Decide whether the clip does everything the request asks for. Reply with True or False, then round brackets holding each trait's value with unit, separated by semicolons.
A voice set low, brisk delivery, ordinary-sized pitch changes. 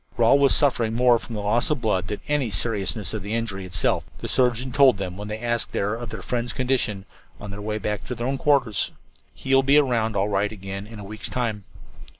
True (110 Hz; 225 wpm; 3.3 semitones)